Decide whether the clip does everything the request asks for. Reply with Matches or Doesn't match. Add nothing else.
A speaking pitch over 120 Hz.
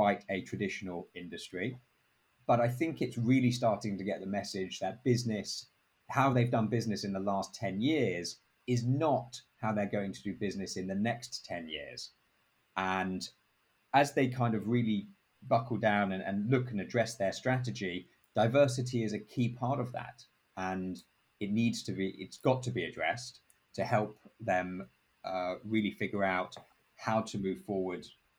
Doesn't match